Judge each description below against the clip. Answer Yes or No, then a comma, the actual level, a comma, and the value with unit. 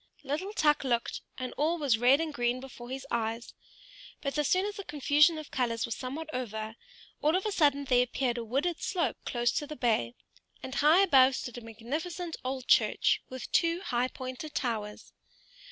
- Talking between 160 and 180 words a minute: No, average, 190 wpm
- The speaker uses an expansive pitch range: No, average, 4.2 semitones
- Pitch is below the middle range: No, very high, 265 Hz